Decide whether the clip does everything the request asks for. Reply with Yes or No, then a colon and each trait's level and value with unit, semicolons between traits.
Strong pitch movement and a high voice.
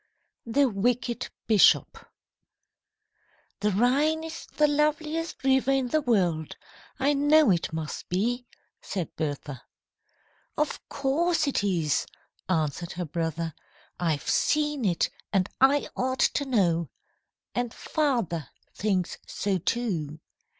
Yes: wide, 8.7 semitones; high, 230 Hz